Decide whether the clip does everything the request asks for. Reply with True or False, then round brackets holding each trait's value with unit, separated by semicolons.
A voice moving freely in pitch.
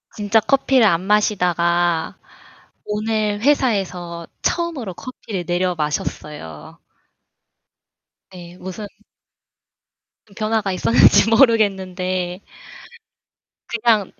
False (3.9 semitones)